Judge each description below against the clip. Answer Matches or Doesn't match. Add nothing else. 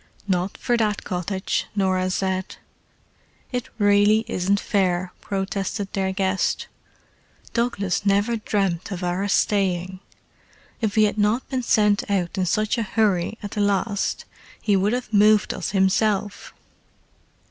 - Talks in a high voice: Matches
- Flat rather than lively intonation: Matches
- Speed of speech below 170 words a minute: Matches